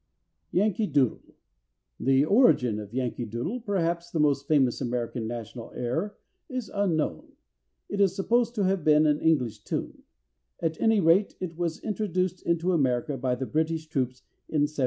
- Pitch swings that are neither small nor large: No, wide, 6.6 semitones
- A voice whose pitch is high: No, medium, 155 Hz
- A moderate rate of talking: Yes, average, 155 wpm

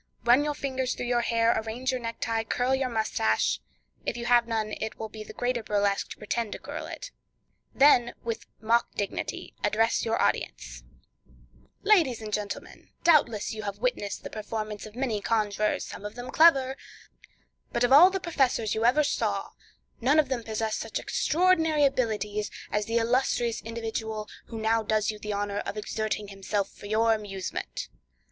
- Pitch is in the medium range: No, high, 225 Hz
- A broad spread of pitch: No, average, 2.9 semitones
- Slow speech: No, average, 170 wpm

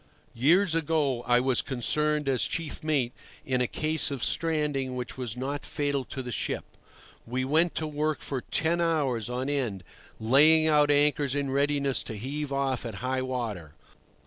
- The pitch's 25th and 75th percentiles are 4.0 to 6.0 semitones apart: No, average, 3.1 semitones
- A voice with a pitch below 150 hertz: Yes, medium, 140 Hz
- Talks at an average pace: Yes, average, 170 wpm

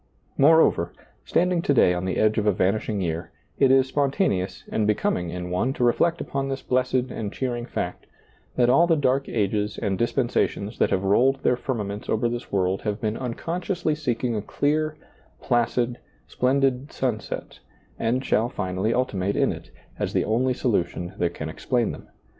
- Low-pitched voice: Yes, low, 120 Hz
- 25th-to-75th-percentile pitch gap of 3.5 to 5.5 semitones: Yes, average, 4.8 semitones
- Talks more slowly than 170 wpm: No, average, 175 wpm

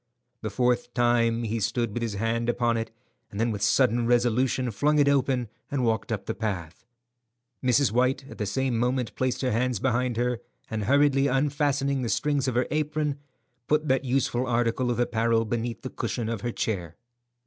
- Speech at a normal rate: Yes, average, 185 wpm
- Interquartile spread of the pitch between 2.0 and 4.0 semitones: Yes, narrow, 2.5 semitones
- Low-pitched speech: Yes, low, 120 Hz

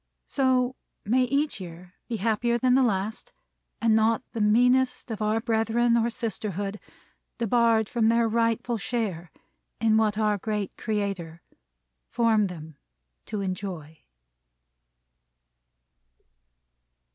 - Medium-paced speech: No, slow, 110 wpm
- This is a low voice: No, high, 220 Hz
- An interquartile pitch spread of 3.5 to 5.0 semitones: No, average, 2.8 semitones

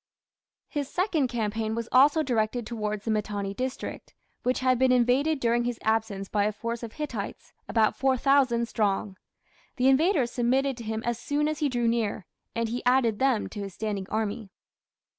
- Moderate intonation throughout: Yes, average, 3.3 semitones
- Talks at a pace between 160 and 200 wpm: Yes, average, 175 wpm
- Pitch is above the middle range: Yes, high, 235 Hz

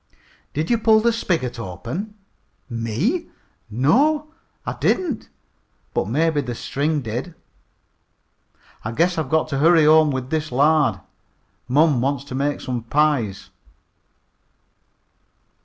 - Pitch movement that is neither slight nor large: Yes, average, 4.9 semitones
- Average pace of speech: No, slow, 120 wpm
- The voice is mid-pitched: Yes, medium, 150 Hz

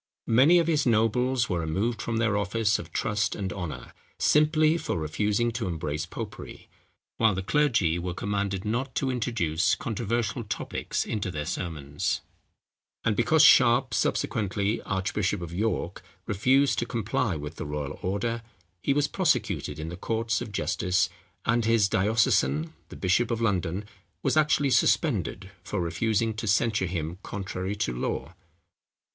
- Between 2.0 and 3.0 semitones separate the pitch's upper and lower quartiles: No, average, 4.5 semitones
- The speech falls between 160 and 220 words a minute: No, average, 150 wpm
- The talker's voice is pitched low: Yes, low, 105 Hz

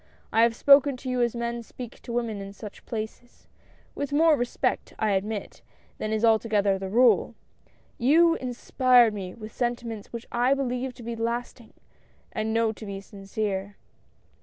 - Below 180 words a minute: Yes, average, 170 wpm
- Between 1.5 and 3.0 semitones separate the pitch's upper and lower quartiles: Yes, narrow, 2.5 semitones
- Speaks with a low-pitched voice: No, high, 235 Hz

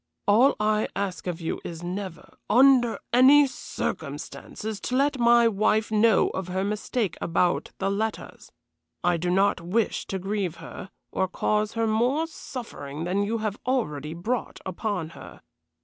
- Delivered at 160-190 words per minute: No, average, 150 wpm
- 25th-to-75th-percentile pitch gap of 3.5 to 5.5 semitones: Yes, average, 4.2 semitones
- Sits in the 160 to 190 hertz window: No, high, 210 Hz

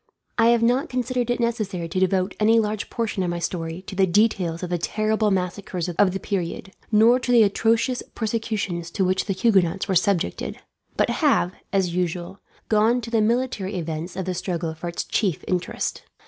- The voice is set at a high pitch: Yes, high, 195 Hz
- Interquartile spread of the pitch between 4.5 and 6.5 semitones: No, average, 4.1 semitones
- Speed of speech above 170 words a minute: Yes, average, 185 wpm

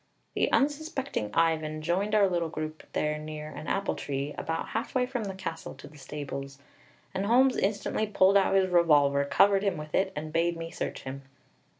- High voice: No, medium, 165 Hz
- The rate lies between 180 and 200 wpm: Yes, average, 185 wpm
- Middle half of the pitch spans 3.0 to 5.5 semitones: Yes, average, 4.6 semitones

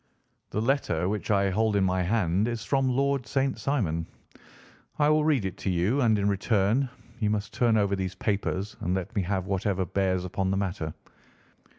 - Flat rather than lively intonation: No, average, 3.9 semitones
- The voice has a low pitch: Yes, low, 100 Hz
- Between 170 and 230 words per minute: Yes, average, 190 wpm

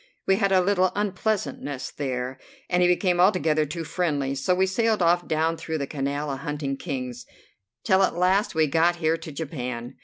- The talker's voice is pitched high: No, medium, 160 Hz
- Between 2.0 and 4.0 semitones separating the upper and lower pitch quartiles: No, average, 4.5 semitones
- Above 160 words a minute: Yes, average, 185 wpm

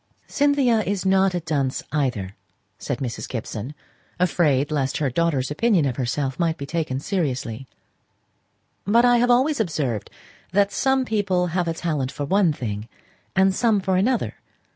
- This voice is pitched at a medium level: Yes, medium, 165 Hz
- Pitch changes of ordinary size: No, wide, 6.9 semitones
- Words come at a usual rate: Yes, average, 155 wpm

